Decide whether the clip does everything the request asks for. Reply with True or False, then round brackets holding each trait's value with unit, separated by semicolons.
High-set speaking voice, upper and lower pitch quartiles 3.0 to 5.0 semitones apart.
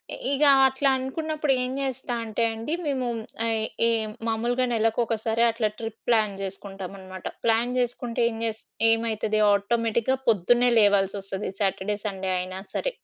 True (225 Hz; 3.3 semitones)